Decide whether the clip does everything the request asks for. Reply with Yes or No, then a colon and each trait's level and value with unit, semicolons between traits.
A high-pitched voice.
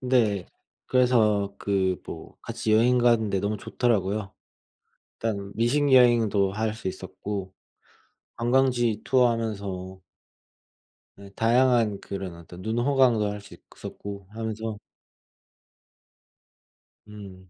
No: low, 110 Hz